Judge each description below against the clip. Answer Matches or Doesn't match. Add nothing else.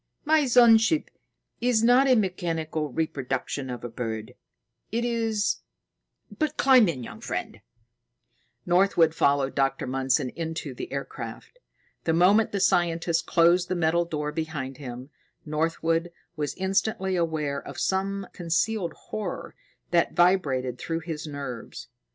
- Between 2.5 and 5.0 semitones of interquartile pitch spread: Doesn't match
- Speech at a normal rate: Doesn't match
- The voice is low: Doesn't match